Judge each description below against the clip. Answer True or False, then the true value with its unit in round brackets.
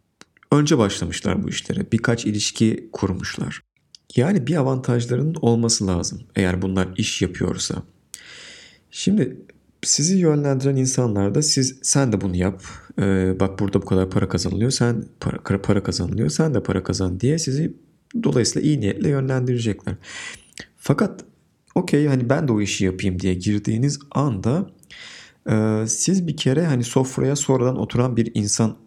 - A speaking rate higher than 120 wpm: True (140 wpm)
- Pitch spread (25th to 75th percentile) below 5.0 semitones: False (5.5 semitones)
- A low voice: True (115 Hz)